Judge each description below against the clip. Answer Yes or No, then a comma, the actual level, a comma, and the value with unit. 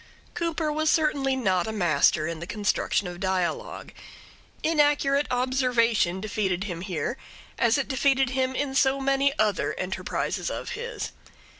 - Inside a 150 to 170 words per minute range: No, average, 140 wpm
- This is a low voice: No, very high, 250 Hz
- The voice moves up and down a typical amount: No, wide, 6.6 semitones